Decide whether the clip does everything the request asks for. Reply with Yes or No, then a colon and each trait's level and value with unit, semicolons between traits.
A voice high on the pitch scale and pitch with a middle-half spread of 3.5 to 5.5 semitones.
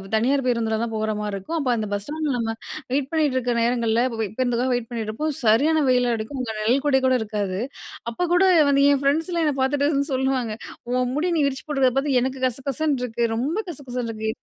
Yes: very high, 255 Hz; average, 3.8 semitones